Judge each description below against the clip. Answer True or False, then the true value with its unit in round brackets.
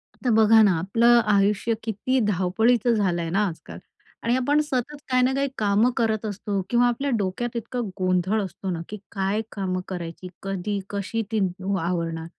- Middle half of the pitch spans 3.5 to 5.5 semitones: True (3.9 semitones)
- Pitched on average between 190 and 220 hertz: True (210 Hz)